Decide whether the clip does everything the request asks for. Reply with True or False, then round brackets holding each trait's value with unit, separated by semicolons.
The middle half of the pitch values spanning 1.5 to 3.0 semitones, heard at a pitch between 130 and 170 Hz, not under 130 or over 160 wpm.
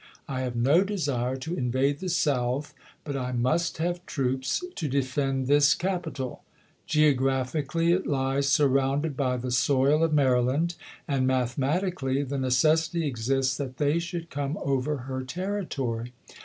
False (3.4 semitones; 140 Hz; 140 wpm)